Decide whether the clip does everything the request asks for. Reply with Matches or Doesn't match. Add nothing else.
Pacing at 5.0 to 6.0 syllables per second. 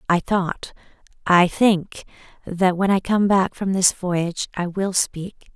Doesn't match